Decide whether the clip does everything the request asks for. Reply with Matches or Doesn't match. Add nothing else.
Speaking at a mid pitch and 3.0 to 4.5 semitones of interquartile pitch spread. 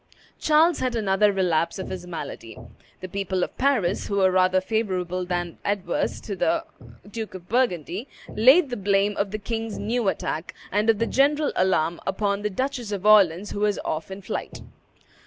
Doesn't match